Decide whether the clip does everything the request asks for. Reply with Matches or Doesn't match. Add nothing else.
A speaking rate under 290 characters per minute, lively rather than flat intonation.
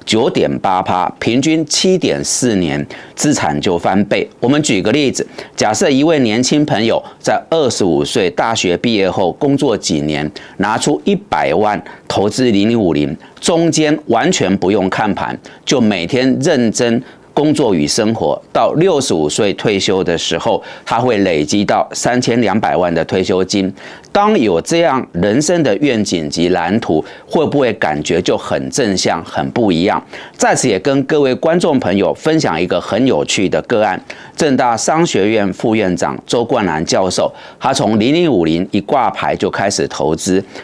Matches